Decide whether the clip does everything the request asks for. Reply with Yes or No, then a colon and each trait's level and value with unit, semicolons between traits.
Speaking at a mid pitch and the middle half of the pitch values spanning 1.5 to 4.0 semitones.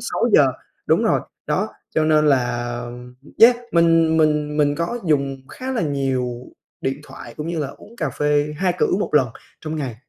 Yes: medium, 150 Hz; average, 3.4 semitones